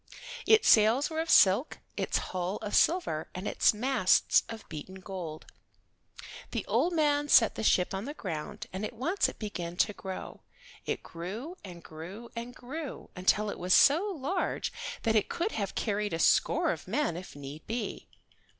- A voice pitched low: No, high, 210 Hz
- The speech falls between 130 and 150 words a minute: No, average, 175 wpm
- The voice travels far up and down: Yes, wide, 6.7 semitones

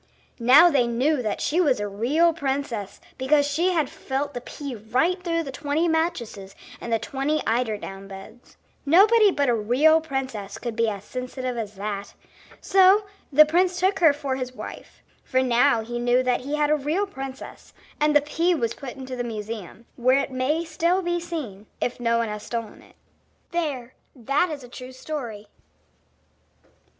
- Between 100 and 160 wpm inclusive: No, average, 180 wpm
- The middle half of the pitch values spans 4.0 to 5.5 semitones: Yes, average, 5.0 semitones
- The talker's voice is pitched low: No, very high, 265 Hz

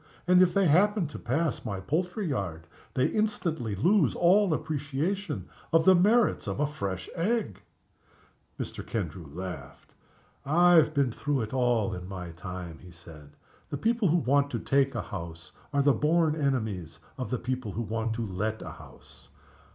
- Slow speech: No, average, 170 wpm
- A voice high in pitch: No, low, 135 Hz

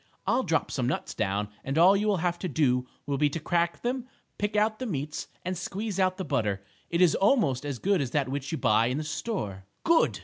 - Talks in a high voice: No, medium, 165 Hz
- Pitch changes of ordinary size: No, wide, 6.7 semitones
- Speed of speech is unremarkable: No, fast, 235 wpm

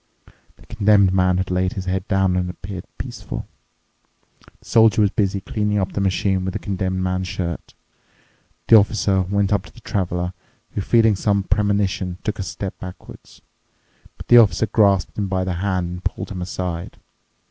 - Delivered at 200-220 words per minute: No, average, 175 wpm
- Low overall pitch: Yes, very low, 95 Hz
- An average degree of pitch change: No, narrow, 1.8 semitones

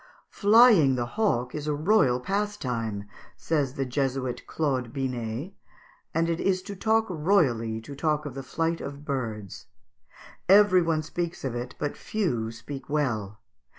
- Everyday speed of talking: Yes, average, 150 wpm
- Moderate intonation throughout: No, wide, 5.9 semitones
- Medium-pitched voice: Yes, medium, 145 Hz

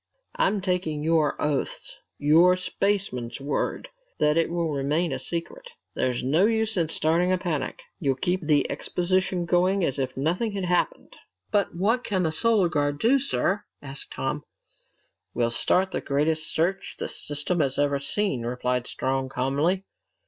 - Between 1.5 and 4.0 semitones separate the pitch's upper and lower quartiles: No, average, 4.8 semitones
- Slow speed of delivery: No, average, 155 wpm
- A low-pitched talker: No, medium, 165 Hz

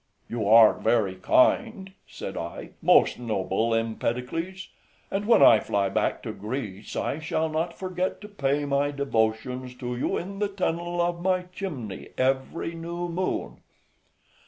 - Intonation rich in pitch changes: Yes, wide, 7.7 semitones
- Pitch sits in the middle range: Yes, medium, 145 Hz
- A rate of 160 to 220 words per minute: No, average, 145 wpm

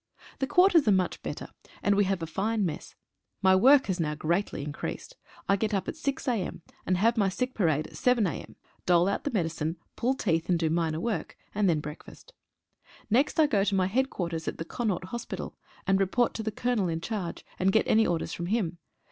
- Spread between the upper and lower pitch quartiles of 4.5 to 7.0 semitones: Yes, average, 5.2 semitones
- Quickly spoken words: Yes, fast, 215 wpm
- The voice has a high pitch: Yes, high, 195 Hz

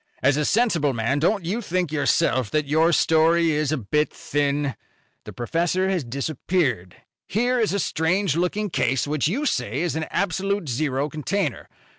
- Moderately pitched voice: Yes, medium, 160 Hz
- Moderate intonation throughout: Yes, average, 4.5 semitones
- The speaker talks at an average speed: Yes, average, 165 wpm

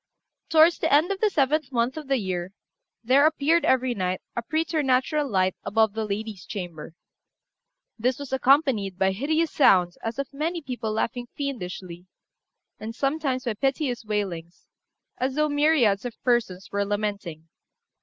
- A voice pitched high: Yes, high, 245 Hz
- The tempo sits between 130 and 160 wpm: Yes, average, 150 wpm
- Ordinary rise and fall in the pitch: No, wide, 6.2 semitones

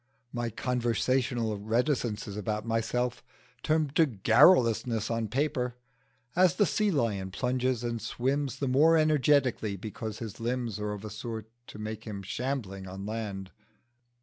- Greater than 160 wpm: No, average, 140 wpm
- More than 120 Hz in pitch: No, low, 115 Hz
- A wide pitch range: No, average, 3.4 semitones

